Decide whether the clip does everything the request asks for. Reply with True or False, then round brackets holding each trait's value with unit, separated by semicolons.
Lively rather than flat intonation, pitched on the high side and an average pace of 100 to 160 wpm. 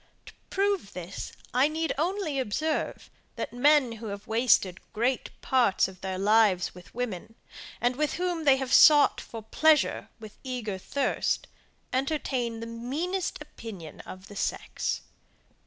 True (6.3 semitones; 245 Hz; 140 wpm)